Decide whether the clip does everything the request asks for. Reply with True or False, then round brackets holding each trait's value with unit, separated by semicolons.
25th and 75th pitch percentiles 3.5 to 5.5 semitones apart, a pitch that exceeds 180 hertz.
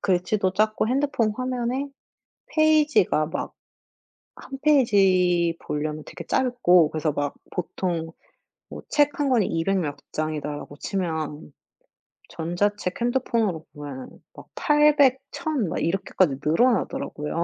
False (7.8 semitones; 190 Hz)